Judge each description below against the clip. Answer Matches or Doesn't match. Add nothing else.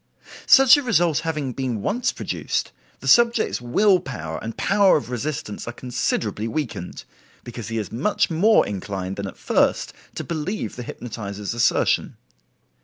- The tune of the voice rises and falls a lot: Matches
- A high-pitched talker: Doesn't match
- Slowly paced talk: Doesn't match